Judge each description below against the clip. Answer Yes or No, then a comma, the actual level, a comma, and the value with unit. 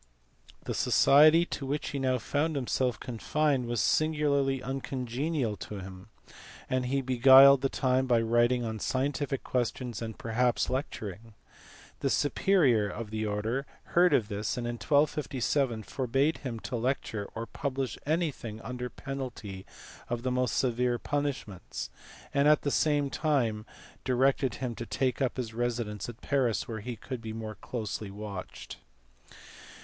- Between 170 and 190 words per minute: No, average, 150 wpm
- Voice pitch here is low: Yes, low, 125 Hz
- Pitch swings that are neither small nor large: Yes, average, 3.4 semitones